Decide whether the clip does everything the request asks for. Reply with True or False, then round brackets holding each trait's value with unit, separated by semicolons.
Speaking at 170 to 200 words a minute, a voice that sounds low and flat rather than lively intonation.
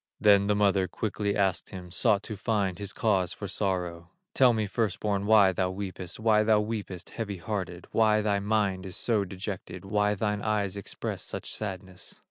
True (180 wpm; 100 Hz; 2.2 semitones)